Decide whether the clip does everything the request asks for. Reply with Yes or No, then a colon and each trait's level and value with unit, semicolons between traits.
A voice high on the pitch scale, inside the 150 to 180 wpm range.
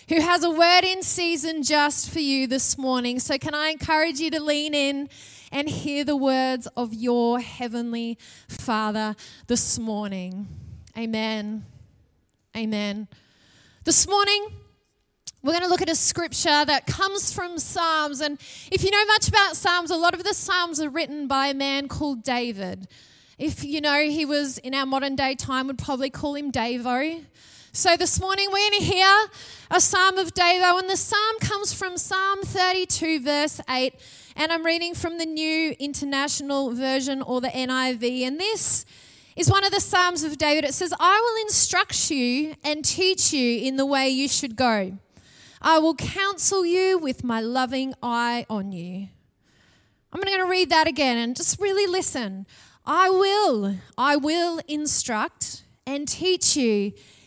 Yes: very high, 295 Hz; average, 170 wpm